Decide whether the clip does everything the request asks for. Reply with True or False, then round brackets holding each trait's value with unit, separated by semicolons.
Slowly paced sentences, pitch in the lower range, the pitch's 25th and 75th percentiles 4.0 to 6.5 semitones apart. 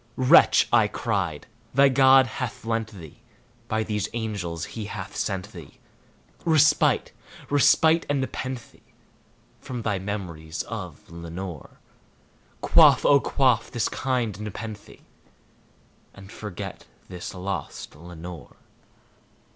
True (105 wpm; 105 Hz; 5.3 semitones)